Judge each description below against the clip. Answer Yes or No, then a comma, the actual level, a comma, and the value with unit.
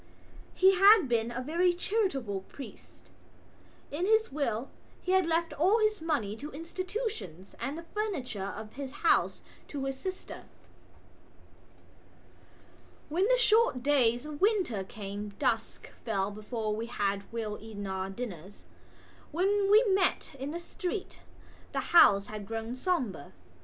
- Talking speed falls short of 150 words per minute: Yes, slow, 135 wpm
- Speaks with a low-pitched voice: No, very high, 275 Hz